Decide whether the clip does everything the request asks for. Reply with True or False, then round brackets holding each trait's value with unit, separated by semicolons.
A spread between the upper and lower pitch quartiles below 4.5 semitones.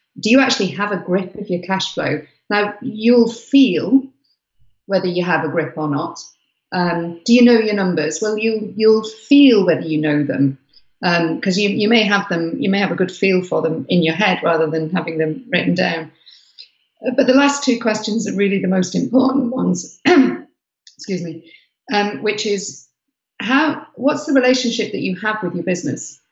False (5.4 semitones)